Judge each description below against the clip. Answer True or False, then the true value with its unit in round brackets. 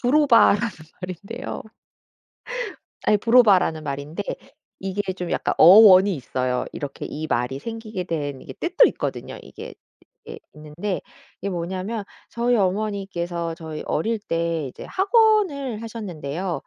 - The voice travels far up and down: True (5.9 semitones)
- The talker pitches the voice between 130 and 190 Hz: True (185 Hz)